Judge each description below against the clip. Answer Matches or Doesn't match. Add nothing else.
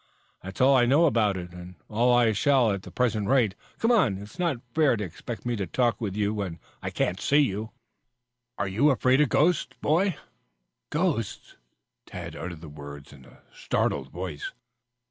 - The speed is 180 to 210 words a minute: Matches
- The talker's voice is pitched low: Matches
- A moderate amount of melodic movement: Doesn't match